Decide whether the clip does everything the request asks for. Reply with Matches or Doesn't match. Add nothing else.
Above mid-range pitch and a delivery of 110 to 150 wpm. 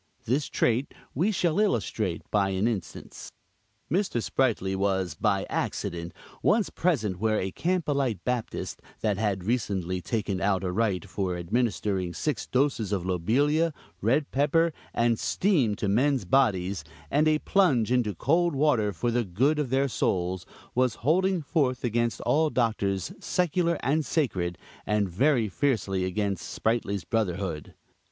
Doesn't match